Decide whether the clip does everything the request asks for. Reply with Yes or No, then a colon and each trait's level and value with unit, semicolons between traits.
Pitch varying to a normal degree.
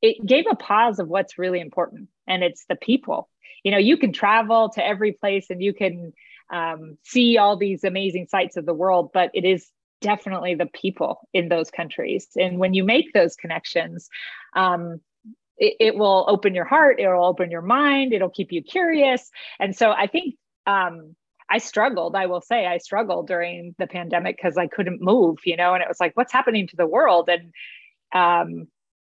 Yes: average, 3.7 semitones